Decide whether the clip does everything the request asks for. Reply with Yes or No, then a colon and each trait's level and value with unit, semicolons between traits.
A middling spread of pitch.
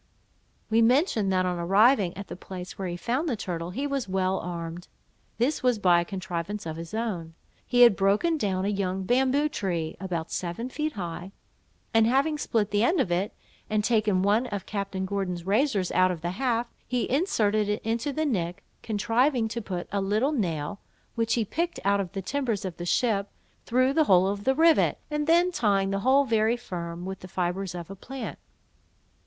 Yes: average, 5.0 semitones